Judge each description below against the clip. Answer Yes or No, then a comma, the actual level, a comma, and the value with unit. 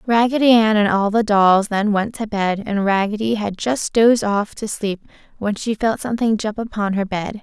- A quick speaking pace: Yes, fast, 210 wpm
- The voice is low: No, high, 215 Hz